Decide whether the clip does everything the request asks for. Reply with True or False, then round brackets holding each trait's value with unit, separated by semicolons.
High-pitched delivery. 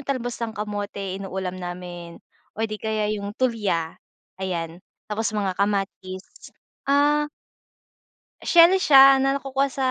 True (210 Hz)